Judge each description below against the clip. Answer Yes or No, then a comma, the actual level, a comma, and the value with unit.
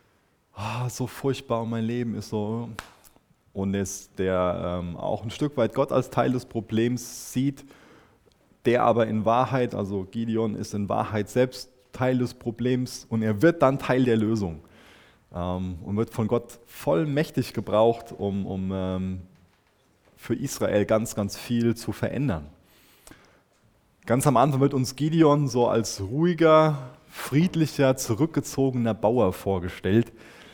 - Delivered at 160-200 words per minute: No, average, 140 wpm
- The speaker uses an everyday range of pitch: Yes, average, 3.9 semitones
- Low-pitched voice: Yes, low, 115 Hz